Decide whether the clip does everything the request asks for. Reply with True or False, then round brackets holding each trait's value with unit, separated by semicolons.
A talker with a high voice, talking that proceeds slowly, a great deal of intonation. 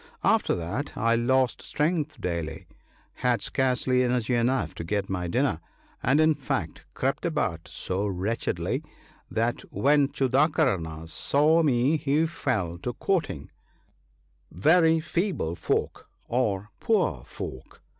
False (125 Hz; 125 wpm; 8.0 semitones)